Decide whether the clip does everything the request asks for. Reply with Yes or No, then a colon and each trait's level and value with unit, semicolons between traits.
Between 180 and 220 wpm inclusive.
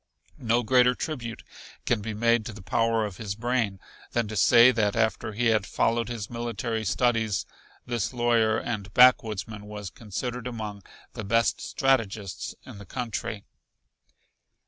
No: average, 145 wpm